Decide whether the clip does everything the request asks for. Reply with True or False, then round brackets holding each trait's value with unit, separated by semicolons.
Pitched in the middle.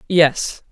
True (160 Hz)